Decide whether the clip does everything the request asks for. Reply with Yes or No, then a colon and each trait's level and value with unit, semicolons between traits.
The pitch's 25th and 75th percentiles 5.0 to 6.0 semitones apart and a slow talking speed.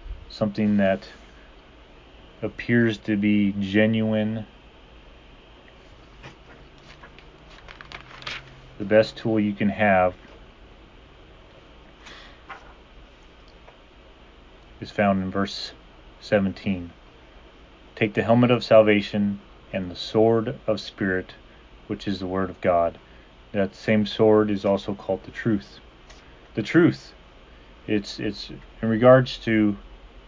Yes: average, 5.3 semitones; slow, 95 wpm